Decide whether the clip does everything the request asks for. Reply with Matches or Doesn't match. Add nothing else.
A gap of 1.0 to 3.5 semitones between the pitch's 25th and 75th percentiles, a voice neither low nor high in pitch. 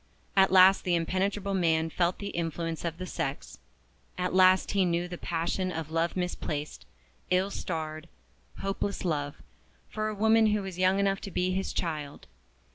Matches